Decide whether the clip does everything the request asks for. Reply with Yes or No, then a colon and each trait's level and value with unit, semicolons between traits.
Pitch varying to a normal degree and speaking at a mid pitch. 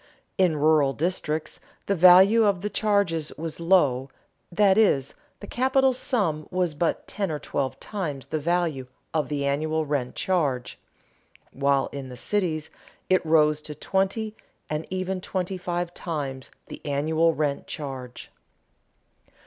Yes: average, 4.4 semitones; medium, 160 Hz